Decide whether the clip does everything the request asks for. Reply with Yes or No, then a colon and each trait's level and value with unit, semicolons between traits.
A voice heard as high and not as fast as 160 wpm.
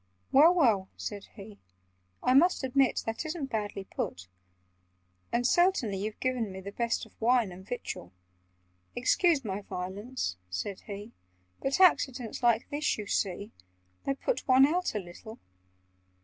Yes: high, 230 Hz; average, 145 wpm